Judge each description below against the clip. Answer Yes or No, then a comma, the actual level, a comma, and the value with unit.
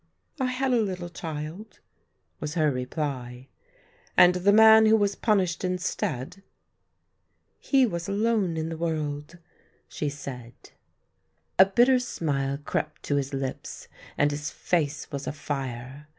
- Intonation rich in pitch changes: Yes, wide, 5.9 semitones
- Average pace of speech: Yes, average, 145 wpm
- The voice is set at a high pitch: No, medium, 165 Hz